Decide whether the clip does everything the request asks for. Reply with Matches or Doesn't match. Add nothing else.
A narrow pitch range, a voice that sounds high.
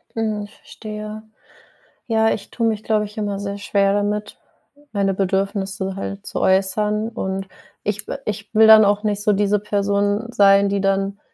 Matches